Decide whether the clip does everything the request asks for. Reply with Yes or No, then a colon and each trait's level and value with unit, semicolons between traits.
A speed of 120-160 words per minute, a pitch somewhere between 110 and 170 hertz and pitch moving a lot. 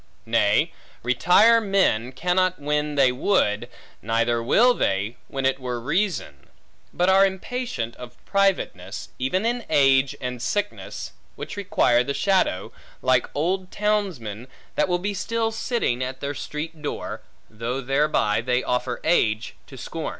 Yes: average, 140 wpm; medium, 140 Hz; wide, 7.7 semitones